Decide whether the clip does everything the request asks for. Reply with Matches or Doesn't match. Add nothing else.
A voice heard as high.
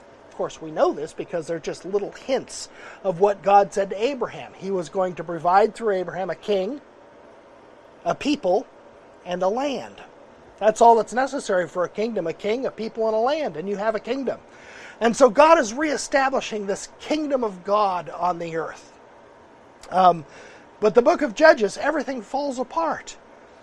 Matches